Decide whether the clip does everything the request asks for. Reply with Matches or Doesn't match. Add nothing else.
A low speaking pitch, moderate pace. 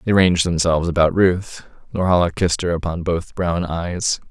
Matches